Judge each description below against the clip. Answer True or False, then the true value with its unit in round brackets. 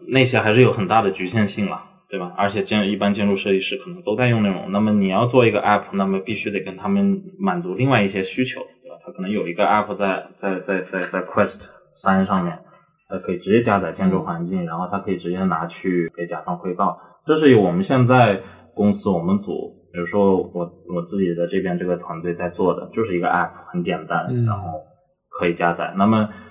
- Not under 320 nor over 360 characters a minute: True (345 characters per minute)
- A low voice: True (100 Hz)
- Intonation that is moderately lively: True (4.2 semitones)